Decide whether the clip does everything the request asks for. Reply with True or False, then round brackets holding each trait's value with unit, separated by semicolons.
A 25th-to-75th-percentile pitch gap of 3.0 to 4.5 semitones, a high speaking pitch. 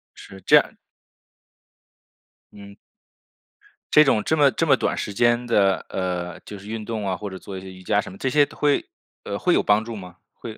False (3.7 semitones; 105 Hz)